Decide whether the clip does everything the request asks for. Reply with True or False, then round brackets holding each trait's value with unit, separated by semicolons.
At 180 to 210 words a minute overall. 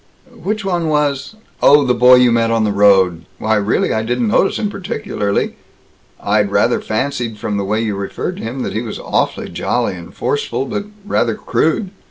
True (190 wpm)